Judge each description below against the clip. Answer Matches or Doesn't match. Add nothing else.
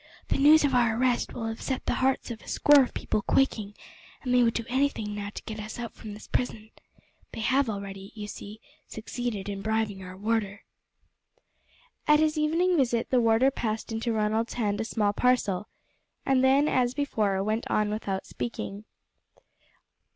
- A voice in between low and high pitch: Doesn't match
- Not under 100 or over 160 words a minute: Doesn't match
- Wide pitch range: Doesn't match